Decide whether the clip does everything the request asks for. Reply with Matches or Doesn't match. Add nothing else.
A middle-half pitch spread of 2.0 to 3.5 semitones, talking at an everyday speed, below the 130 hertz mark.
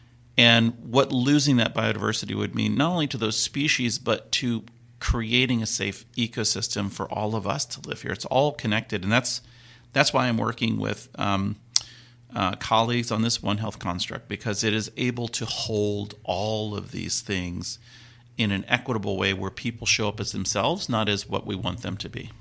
Matches